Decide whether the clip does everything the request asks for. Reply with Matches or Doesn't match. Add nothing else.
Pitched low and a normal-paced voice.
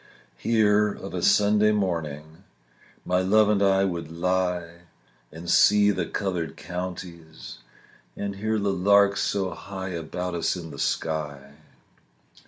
Doesn't match